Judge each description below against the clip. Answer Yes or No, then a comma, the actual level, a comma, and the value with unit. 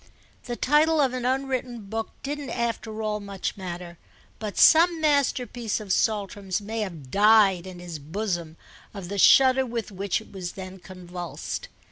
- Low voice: No, high, 210 Hz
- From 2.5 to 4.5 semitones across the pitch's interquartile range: No, average, 5.0 semitones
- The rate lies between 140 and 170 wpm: Yes, average, 155 wpm